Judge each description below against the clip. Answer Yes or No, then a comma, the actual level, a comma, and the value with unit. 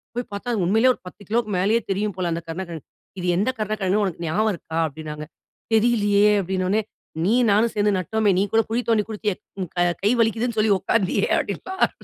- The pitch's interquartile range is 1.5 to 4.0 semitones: Yes, average, 3.2 semitones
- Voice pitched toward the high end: Yes, high, 205 Hz